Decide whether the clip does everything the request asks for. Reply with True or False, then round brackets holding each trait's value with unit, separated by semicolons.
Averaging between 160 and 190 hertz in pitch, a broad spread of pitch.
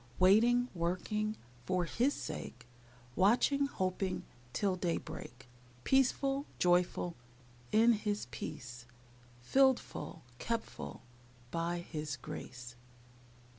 True (185 Hz; 5.9 semitones)